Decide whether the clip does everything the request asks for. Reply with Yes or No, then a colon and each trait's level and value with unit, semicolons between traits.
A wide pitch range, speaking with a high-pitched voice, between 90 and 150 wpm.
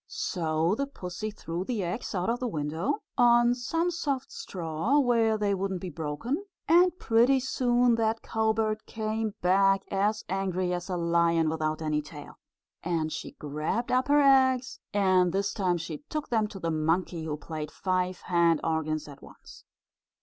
No: wide, 6.1 semitones; high, 195 Hz; average, 165 wpm